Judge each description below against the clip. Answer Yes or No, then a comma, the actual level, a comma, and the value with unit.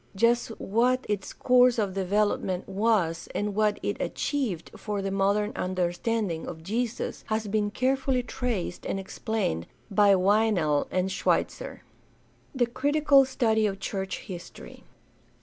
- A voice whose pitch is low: No, high, 210 Hz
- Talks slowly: Yes, slow, 130 wpm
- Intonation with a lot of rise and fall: No, average, 3.7 semitones